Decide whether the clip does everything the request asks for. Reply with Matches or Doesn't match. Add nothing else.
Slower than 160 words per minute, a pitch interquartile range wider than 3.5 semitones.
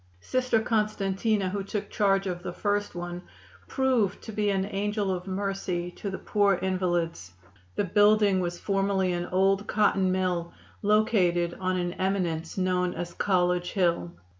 Doesn't match